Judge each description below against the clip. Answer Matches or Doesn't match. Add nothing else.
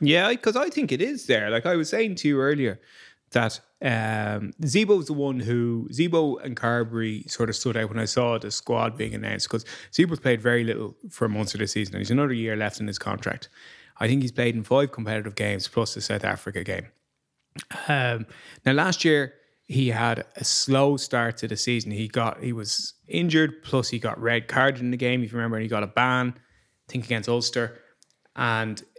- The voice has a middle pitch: Doesn't match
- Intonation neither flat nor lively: Matches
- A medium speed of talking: Doesn't match